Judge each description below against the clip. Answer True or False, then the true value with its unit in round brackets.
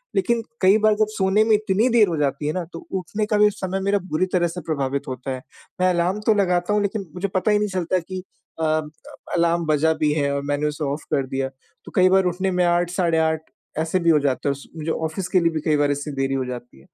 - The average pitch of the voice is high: False (175 Hz)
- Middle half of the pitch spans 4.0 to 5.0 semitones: True (4.3 semitones)